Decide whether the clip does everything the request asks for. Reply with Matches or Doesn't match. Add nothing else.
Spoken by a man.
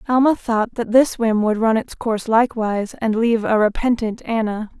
Doesn't match